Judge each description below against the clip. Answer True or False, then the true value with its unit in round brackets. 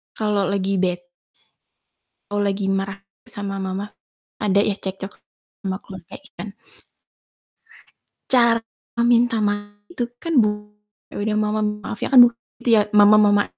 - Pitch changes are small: True (1.5 semitones)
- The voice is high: True (205 Hz)